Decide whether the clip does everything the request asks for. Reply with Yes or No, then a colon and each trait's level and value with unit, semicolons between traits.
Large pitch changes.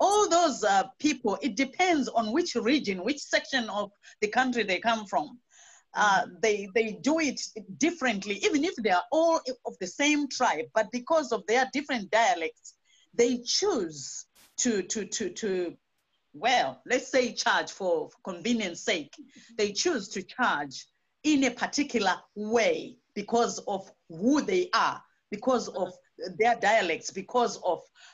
Yes: wide, 5.7 semitones